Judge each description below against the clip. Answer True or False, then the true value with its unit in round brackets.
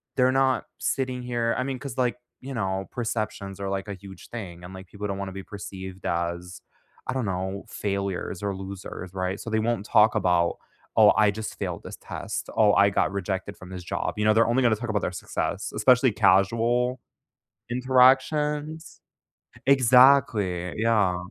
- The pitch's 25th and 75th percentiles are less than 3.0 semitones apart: False (4.5 semitones)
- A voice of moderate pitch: False (105 Hz)